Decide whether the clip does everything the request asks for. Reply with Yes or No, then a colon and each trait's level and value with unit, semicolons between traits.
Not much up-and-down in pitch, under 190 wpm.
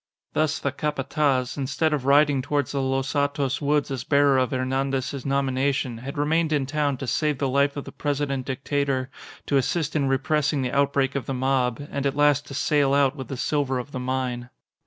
No: narrow, 1.6 semitones; average, 200 wpm